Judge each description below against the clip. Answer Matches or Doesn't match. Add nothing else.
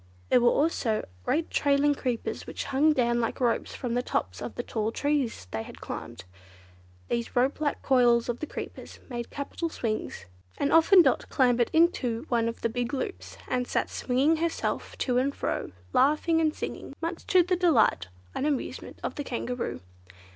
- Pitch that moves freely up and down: Doesn't match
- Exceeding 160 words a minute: Matches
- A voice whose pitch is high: Matches